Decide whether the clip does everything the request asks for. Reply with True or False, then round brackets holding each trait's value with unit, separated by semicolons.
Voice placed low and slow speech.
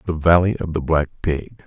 False (80 Hz; 215 wpm)